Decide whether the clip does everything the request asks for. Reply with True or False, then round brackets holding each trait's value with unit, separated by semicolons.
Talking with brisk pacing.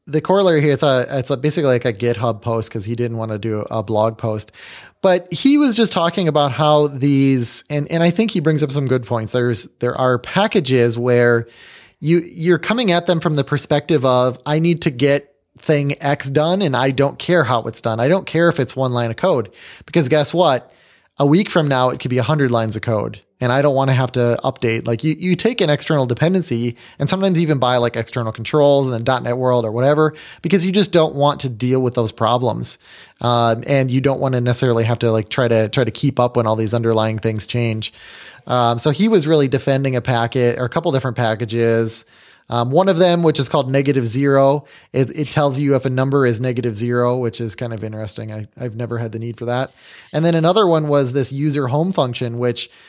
True (235 wpm)